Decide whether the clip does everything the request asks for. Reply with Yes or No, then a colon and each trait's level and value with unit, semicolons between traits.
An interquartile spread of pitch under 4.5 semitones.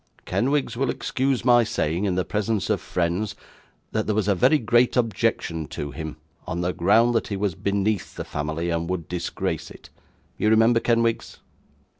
No: average, 5.0 semitones